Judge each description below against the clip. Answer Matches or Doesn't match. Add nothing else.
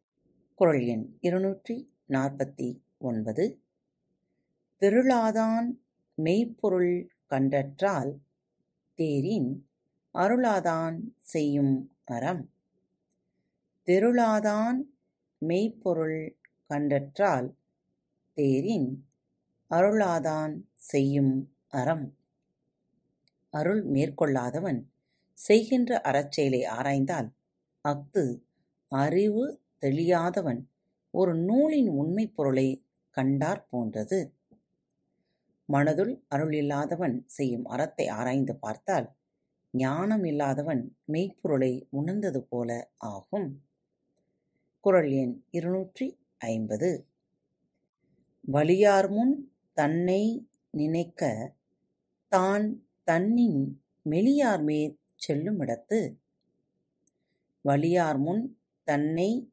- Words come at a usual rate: Doesn't match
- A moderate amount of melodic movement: Doesn't match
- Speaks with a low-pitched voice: Doesn't match